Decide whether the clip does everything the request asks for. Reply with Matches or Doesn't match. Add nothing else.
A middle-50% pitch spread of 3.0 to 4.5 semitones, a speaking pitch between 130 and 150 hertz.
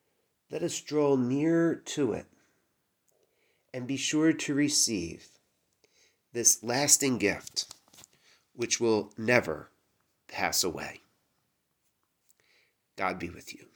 Matches